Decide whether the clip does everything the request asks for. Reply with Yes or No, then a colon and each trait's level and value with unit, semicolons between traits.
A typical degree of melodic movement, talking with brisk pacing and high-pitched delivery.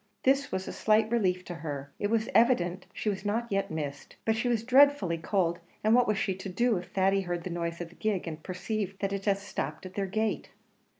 Yes: average, 3.8 semitones; fast, 235 wpm; high, 195 Hz